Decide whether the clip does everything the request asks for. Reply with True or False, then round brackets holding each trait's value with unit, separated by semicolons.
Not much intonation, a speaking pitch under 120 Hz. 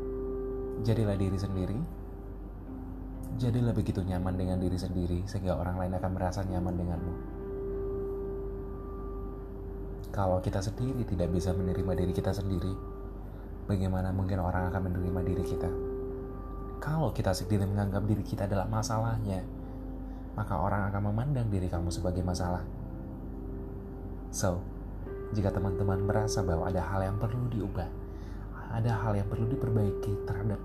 True (1.9 semitones; 95 Hz)